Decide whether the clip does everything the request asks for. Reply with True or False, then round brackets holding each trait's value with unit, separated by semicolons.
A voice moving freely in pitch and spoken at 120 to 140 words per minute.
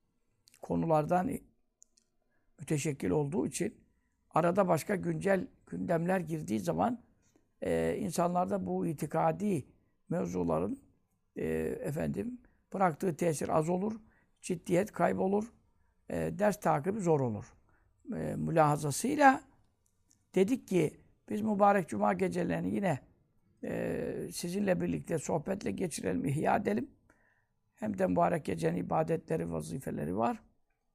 False (5.8 semitones; 100 wpm)